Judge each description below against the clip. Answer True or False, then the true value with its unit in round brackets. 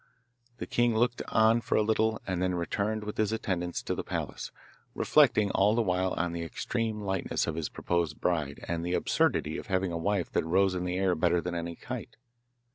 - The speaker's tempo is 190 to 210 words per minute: True (205 wpm)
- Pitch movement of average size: True (3.8 semitones)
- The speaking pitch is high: False (95 Hz)